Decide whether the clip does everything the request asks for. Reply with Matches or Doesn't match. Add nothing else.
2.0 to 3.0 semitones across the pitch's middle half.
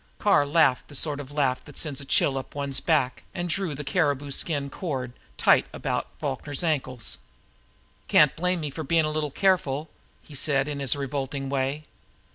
Matches